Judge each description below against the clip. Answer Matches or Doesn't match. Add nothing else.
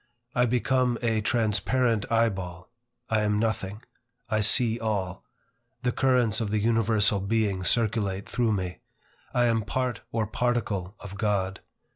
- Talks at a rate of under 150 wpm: Matches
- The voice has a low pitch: Matches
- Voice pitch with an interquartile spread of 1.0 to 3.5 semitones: Matches